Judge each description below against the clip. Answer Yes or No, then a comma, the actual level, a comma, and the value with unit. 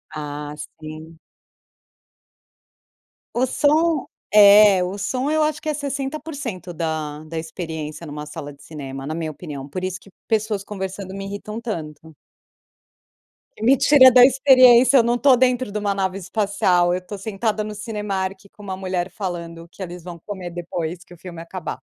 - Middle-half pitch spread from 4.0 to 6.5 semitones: Yes, wide, 5.5 semitones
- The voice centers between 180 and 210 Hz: Yes, high, 190 Hz